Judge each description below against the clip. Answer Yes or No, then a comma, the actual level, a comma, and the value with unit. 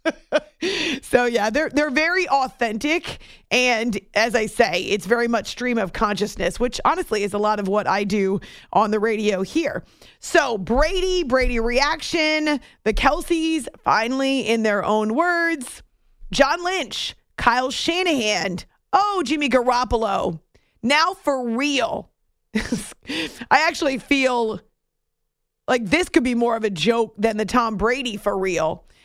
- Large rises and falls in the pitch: Yes, wide, 5.9 semitones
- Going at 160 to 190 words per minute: No, average, 140 wpm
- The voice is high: Yes, high, 245 Hz